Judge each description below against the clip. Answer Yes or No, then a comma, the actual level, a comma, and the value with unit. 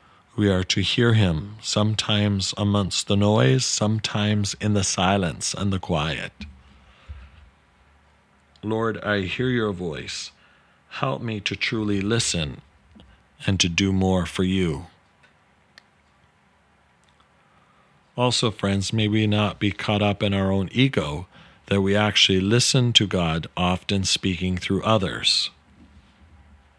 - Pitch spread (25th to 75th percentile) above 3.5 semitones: No, average, 2.8 semitones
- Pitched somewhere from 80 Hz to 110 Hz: Yes, low, 100 Hz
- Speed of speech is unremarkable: No, slow, 120 wpm